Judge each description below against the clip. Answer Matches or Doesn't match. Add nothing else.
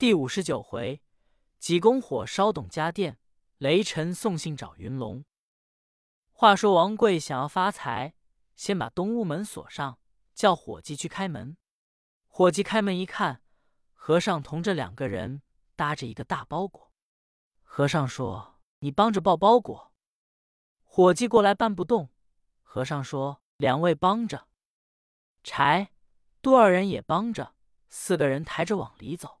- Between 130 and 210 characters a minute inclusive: Matches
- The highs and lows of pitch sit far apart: Matches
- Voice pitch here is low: Doesn't match